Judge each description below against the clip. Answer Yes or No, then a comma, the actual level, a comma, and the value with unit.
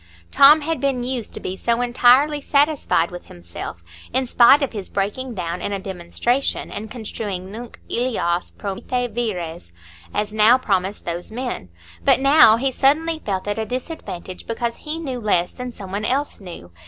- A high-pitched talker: Yes, high, 230 Hz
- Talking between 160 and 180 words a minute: Yes, average, 170 wpm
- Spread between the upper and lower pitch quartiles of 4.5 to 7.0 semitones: Yes, wide, 5.4 semitones